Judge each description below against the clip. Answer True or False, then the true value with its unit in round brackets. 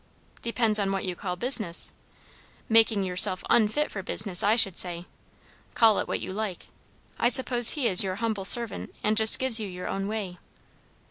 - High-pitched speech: True (210 Hz)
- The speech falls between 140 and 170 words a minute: False (180 wpm)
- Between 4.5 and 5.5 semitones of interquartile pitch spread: False (3.4 semitones)